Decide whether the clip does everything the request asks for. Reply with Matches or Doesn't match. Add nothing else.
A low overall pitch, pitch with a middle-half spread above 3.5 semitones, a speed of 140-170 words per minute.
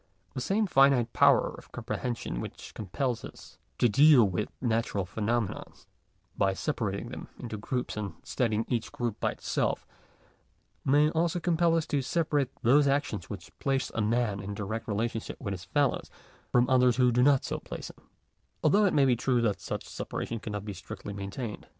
Doesn't match